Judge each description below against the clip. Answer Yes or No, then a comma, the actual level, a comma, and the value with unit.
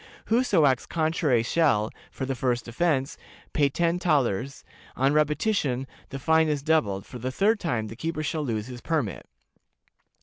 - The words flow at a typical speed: Yes, average, 160 wpm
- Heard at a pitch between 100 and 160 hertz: Yes, medium, 140 Hz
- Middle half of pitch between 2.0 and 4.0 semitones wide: No, average, 4.7 semitones